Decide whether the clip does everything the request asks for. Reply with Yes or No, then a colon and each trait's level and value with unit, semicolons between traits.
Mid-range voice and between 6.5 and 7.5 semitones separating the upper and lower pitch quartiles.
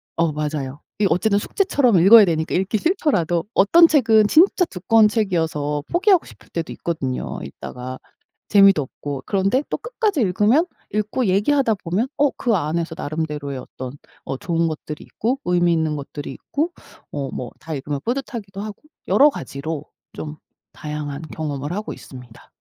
Yes: medium, 175 Hz; wide, 7.1 semitones